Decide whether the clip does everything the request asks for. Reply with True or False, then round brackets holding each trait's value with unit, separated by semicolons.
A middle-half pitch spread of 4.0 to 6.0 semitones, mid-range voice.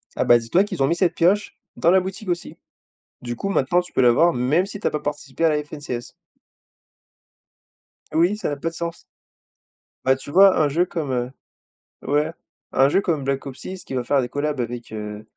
True (5.2 semitones; 150 Hz)